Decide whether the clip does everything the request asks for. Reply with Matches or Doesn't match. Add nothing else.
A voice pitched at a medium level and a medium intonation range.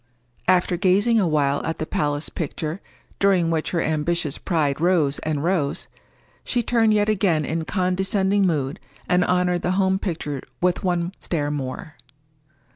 Matches